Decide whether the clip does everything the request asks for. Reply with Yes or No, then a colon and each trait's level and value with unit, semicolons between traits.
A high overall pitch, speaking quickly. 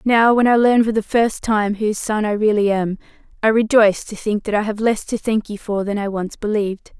Yes: high, 215 Hz; fast, 250 wpm